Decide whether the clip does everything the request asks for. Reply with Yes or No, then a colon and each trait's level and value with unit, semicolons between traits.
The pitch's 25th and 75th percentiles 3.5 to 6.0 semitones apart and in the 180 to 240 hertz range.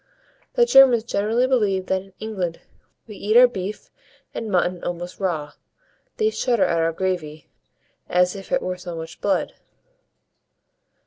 Yes: average, 4.0 semitones; high, 190 Hz